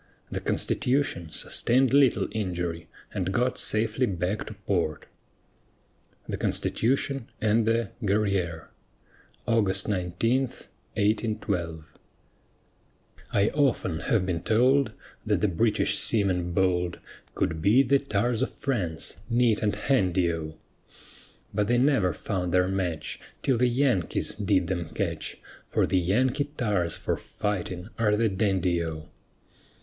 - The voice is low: Yes, low, 100 Hz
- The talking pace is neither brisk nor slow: No, slow, 125 wpm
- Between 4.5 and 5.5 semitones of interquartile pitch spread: Yes, average, 5.0 semitones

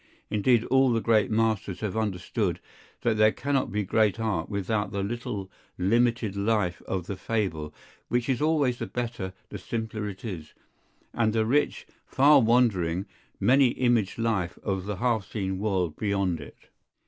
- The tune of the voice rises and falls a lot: No, average, 3.5 semitones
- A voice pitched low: Yes, low, 110 Hz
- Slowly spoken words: No, average, 160 wpm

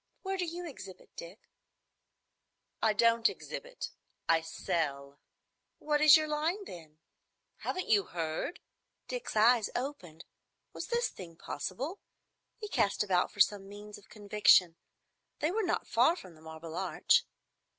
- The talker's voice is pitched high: Yes, high, 210 Hz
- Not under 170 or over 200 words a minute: No, average, 140 wpm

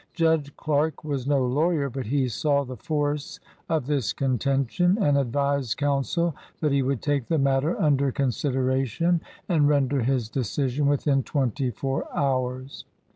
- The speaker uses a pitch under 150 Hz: Yes, medium, 140 Hz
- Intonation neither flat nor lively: No, narrow, 2.1 semitones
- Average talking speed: Yes, average, 150 wpm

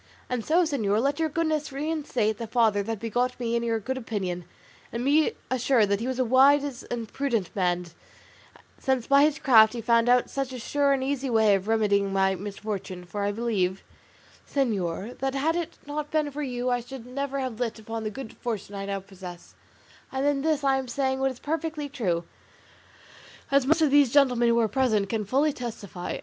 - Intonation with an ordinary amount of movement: Yes, average, 4.7 semitones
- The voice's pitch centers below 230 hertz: No, high, 245 Hz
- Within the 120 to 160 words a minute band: No, average, 200 wpm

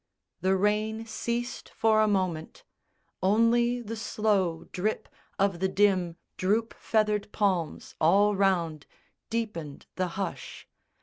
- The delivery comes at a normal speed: No, slow, 115 wpm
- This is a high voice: Yes, high, 205 Hz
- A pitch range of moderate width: Yes, average, 3.0 semitones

